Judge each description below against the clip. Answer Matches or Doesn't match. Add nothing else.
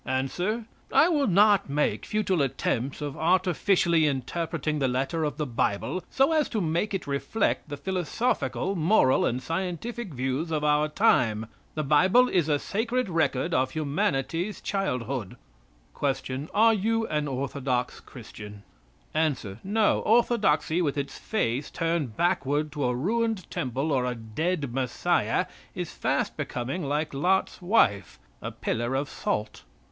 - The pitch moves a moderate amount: Doesn't match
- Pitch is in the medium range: Matches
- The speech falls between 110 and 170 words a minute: Matches